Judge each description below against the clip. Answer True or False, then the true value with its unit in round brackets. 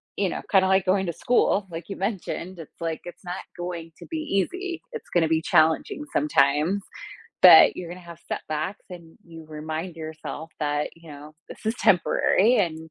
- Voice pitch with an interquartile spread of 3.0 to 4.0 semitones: True (3.4 semitones)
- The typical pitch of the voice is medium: True (175 Hz)